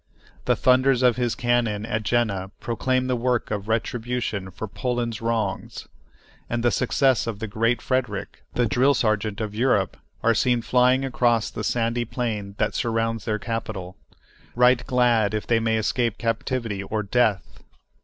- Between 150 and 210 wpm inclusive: Yes, average, 155 wpm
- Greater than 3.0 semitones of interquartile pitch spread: No, narrow, 2.4 semitones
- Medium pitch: No, low, 115 Hz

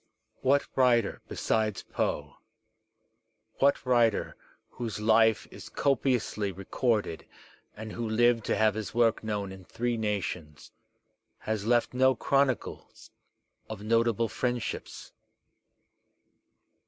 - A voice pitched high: No, low, 115 Hz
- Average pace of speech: No, slow, 105 wpm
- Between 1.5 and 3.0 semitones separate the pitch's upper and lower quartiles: Yes, narrow, 2.4 semitones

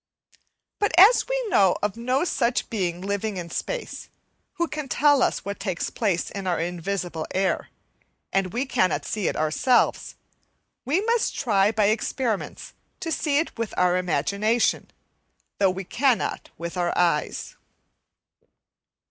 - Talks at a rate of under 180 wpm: Yes, average, 140 wpm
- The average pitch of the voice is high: Yes, high, 205 Hz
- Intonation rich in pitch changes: Yes, wide, 6.7 semitones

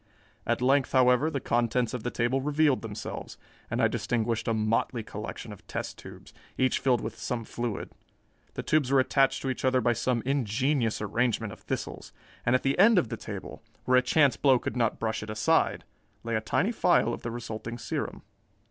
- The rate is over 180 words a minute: Yes, average, 195 wpm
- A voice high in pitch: No, low, 120 Hz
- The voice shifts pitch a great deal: No, average, 2.8 semitones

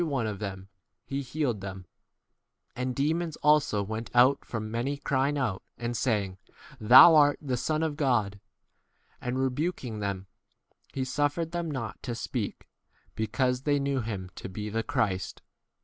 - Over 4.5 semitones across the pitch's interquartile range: Yes, average, 5.0 semitones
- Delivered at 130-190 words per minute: Yes, average, 160 wpm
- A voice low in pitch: Yes, low, 125 Hz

